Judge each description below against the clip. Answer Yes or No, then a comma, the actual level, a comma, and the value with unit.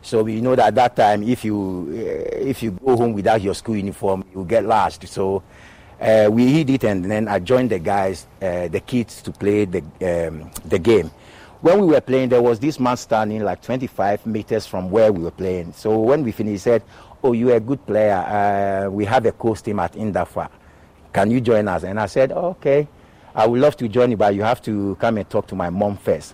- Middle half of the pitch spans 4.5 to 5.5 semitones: No, average, 3.8 semitones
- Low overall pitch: Yes, low, 110 Hz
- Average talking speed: No, fast, 230 wpm